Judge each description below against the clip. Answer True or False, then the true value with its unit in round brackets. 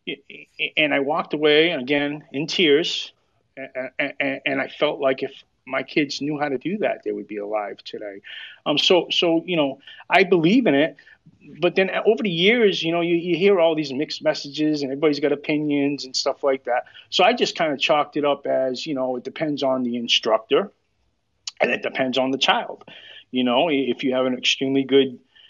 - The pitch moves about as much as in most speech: True (3.6 semitones)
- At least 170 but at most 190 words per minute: False (200 wpm)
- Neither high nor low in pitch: True (145 Hz)